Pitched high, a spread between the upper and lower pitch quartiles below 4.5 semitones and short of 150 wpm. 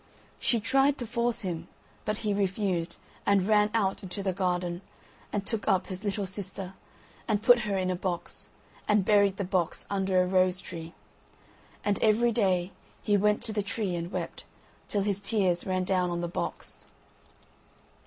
No: high, 195 Hz; narrow, 2.4 semitones; average, 175 wpm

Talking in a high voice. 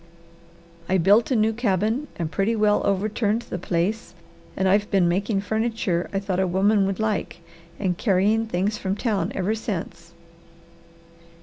Yes: high, 200 Hz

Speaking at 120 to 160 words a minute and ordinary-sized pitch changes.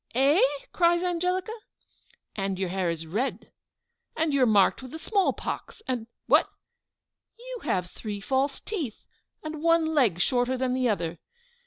No: average, 155 wpm; wide, 8.4 semitones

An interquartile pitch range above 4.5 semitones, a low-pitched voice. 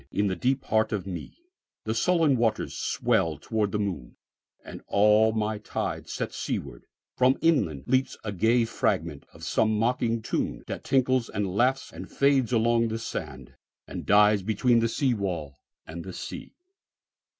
No: average, 3.9 semitones; low, 110 Hz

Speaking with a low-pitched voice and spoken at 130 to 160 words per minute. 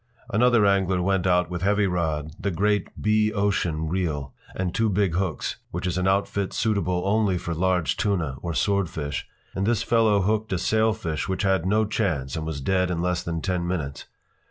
No: very low, 95 Hz; average, 185 wpm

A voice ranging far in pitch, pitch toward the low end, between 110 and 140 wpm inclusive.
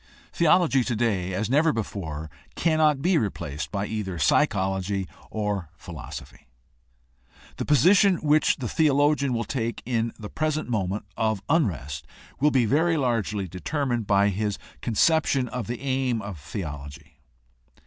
Yes: wide, 6.8 semitones; low, 115 Hz; slow, 135 wpm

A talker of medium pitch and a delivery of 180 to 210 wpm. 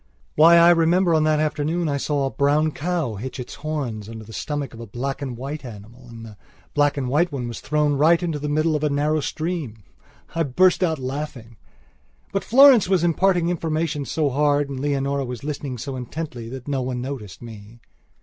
Yes: medium, 145 Hz; average, 200 wpm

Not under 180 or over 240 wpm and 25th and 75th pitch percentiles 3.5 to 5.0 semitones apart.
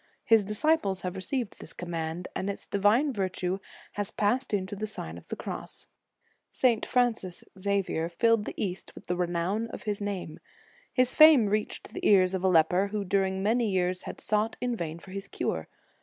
No: average, 185 wpm; average, 3.1 semitones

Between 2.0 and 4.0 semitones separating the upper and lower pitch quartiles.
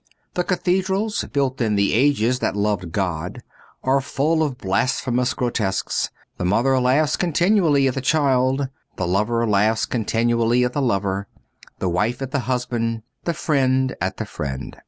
No: average, 4.8 semitones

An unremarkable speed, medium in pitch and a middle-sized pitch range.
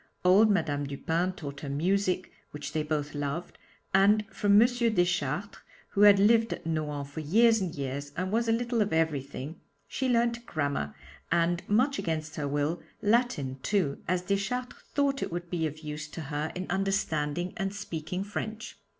No: average, 170 wpm; medium, 175 Hz; wide, 5.7 semitones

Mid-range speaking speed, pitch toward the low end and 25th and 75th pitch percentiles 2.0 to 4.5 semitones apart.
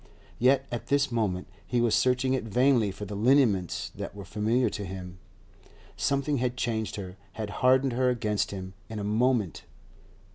Yes: average, 170 wpm; low, 115 Hz; average, 4.0 semitones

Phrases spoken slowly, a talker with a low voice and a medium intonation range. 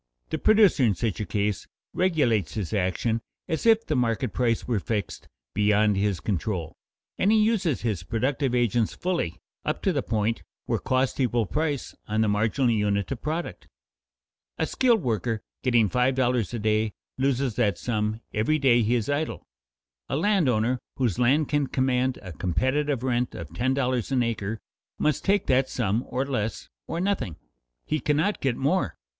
No: average, 170 wpm; low, 120 Hz; average, 4.5 semitones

